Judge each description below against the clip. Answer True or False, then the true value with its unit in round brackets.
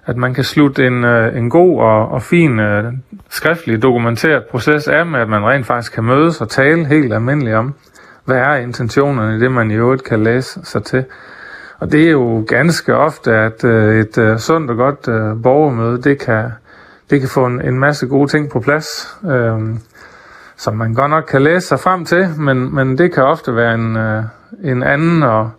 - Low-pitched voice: True (130 Hz)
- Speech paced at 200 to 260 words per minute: False (190 wpm)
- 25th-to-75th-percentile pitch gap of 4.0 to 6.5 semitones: True (4.4 semitones)